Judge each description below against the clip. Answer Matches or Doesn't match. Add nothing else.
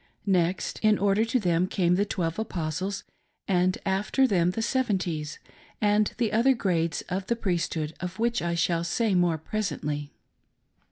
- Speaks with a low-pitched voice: Doesn't match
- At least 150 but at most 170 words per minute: Matches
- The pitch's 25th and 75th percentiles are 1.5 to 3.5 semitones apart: Doesn't match